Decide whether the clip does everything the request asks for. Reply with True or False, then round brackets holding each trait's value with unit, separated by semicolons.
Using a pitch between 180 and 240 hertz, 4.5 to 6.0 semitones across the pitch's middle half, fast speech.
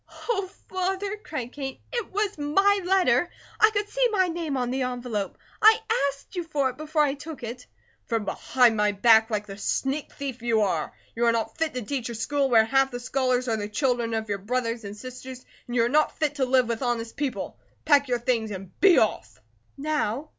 False (255 Hz; 4.9 semitones; 215 wpm)